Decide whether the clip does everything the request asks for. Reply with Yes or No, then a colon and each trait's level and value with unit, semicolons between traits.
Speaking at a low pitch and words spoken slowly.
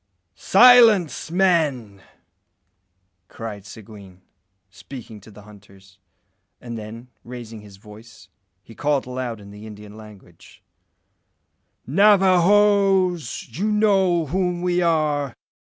Yes: low, 125 Hz; slow, 100 wpm